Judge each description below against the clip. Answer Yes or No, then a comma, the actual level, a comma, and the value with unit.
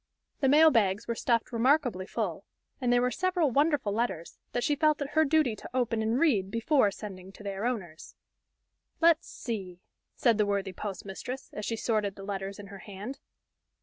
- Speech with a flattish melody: No, average, 5.2 semitones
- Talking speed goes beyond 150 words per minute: Yes, average, 180 wpm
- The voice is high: Yes, high, 225 Hz